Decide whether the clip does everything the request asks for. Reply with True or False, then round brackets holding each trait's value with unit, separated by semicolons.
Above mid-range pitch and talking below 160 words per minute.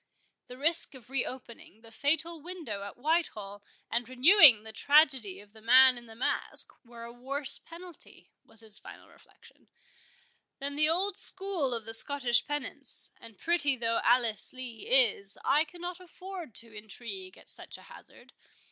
False (255 Hz; 165 wpm)